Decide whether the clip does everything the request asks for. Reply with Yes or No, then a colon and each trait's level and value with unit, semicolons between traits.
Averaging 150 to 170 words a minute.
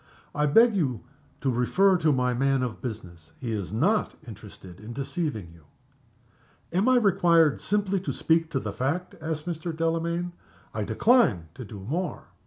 Yes: average, 165 wpm